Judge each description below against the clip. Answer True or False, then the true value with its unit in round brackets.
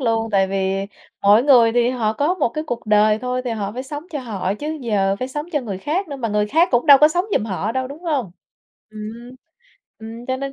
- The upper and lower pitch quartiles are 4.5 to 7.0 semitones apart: True (5.0 semitones)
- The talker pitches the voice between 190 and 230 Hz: False (240 Hz)